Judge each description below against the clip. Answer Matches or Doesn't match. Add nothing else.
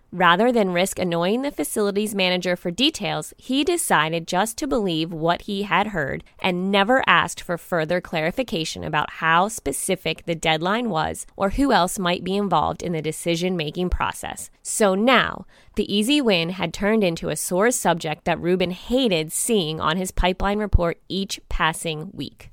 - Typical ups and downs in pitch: Matches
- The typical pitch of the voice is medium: Matches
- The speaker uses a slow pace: Doesn't match